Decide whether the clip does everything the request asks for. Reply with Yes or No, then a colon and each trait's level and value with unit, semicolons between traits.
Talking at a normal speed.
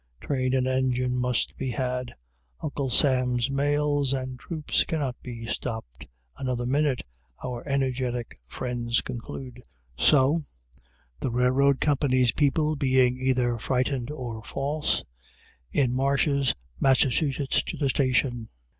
No: slow, 115 wpm